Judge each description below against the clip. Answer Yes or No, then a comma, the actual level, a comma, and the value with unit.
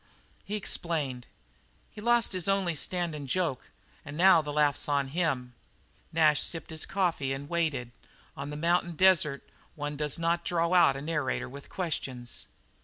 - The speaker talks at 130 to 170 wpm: Yes, average, 155 wpm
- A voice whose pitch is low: No, medium, 160 Hz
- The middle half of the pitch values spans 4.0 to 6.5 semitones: No, average, 3.5 semitones